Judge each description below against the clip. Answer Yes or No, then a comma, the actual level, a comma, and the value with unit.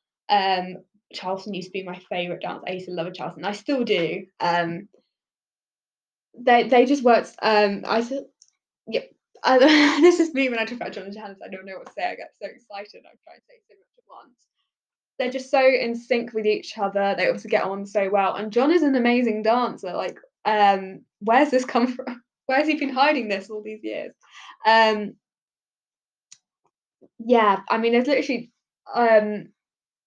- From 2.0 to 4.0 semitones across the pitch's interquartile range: No, average, 4.6 semitones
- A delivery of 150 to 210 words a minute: Yes, average, 190 wpm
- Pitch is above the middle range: Yes, high, 225 Hz